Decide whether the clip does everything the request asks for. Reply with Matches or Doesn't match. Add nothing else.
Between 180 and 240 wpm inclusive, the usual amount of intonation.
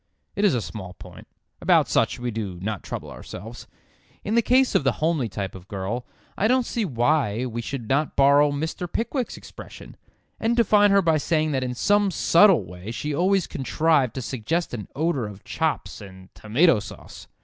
Doesn't match